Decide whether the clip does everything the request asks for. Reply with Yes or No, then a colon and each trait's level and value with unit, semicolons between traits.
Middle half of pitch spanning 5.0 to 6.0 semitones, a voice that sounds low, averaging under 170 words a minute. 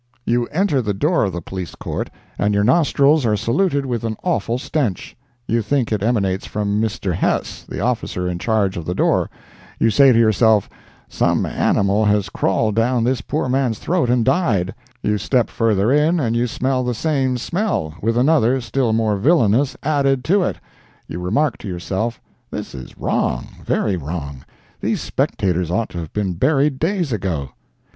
No: average, 5.3 semitones; low, 115 Hz; average, 175 wpm